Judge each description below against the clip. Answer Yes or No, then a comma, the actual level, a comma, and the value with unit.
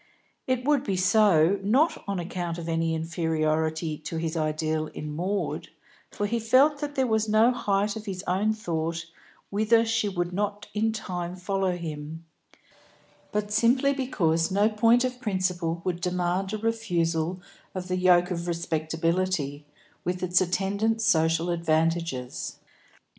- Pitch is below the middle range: No, medium, 180 Hz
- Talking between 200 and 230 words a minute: No, average, 145 wpm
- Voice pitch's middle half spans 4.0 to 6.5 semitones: Yes, average, 4.5 semitones